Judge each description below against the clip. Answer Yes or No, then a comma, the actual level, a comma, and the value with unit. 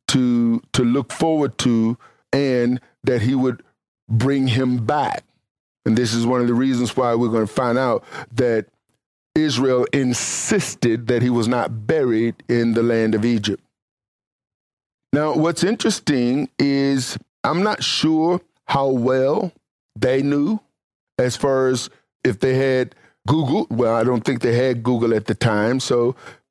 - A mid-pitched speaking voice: No, low, 125 Hz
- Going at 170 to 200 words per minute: No, average, 150 wpm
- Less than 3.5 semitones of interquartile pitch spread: Yes, narrow, 2.6 semitones